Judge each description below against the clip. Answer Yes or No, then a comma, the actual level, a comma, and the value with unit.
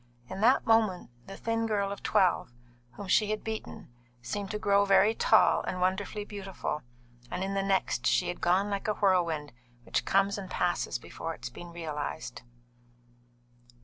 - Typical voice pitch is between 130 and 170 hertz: No, high, 195 Hz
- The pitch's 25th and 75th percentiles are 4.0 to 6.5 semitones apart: No, average, 2.8 semitones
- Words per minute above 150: Yes, average, 170 wpm